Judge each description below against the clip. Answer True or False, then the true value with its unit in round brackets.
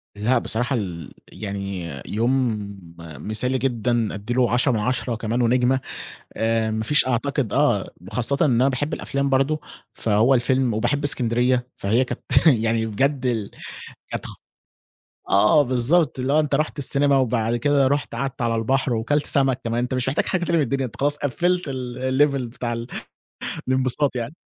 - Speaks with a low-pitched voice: True (125 Hz)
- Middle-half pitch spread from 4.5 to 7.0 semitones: False (3.3 semitones)